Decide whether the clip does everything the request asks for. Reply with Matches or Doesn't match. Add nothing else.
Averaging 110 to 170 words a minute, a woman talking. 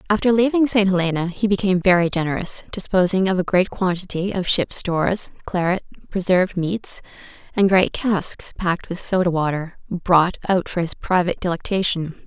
Matches